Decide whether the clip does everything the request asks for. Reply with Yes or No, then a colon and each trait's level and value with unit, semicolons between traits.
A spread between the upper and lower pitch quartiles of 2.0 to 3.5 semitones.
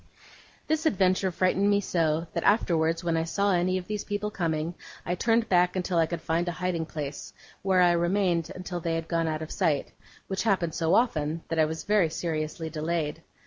Yes: narrow, 2.6 semitones